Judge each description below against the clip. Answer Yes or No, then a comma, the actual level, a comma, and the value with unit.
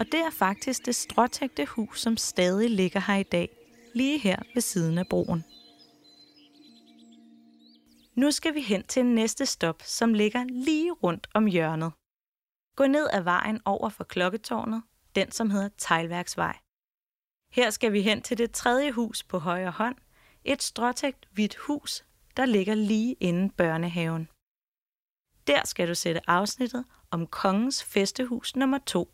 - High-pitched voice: Yes, high, 215 Hz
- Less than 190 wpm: Yes, average, 150 wpm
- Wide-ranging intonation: Yes, wide, 5.9 semitones